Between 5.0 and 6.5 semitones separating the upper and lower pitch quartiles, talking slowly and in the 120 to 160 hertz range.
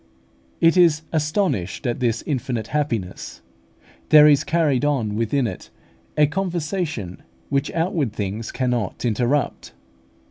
Yes: average, 5.3 semitones; slow, 115 wpm; medium, 140 Hz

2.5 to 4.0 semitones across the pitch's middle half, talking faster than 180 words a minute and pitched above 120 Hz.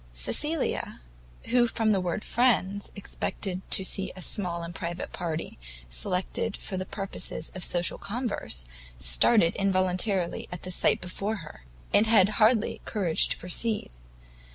No: average, 3.7 semitones; average, 145 wpm; high, 190 Hz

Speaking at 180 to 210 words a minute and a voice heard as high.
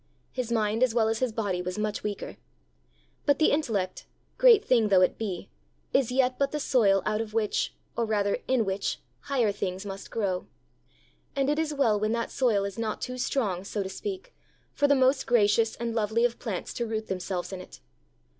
Yes: average, 200 wpm; high, 225 Hz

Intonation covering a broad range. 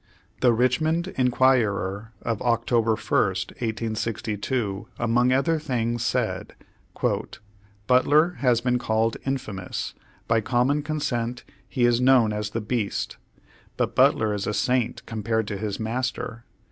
No: narrow, 2.5 semitones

